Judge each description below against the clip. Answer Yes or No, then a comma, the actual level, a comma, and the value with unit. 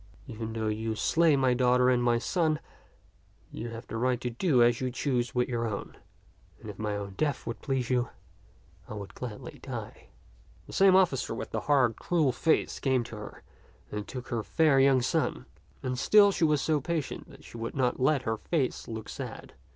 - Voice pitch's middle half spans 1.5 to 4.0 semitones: Yes, average, 3.6 semitones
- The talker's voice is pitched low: Yes, low, 125 Hz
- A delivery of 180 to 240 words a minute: Yes, average, 195 wpm